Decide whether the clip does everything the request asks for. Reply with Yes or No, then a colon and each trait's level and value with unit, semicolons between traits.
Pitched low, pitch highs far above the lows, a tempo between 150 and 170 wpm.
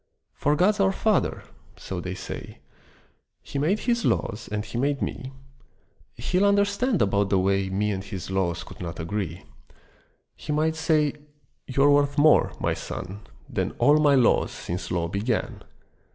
Yes: low, 130 Hz; wide, 8.4 semitones; average, 155 wpm